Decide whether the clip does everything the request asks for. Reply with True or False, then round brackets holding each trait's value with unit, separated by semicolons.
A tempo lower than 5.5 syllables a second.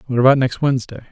False (8.5 syllables/s)